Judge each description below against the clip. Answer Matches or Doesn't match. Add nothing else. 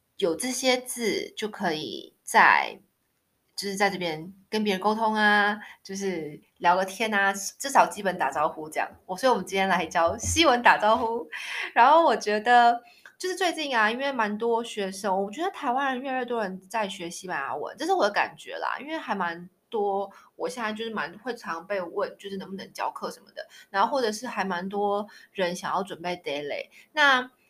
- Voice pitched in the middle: Doesn't match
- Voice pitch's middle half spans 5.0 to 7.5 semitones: Doesn't match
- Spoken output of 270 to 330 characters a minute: Matches